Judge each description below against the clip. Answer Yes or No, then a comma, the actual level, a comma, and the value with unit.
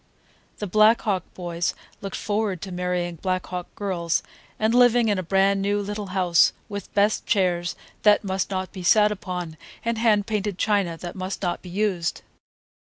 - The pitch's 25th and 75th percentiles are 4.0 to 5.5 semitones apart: No, narrow, 2.6 semitones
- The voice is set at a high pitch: Yes, high, 195 Hz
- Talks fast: No, average, 175 wpm